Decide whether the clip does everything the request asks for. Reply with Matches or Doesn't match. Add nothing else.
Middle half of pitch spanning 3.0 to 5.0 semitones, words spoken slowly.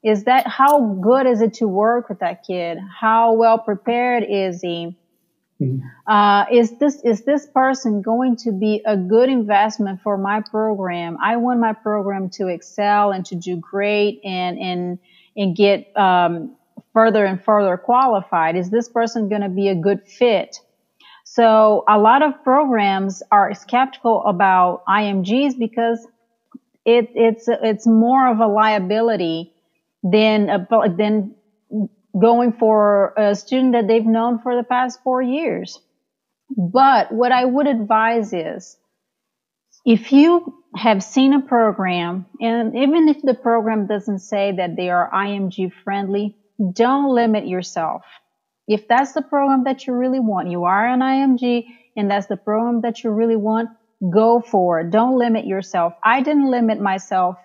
Doesn't match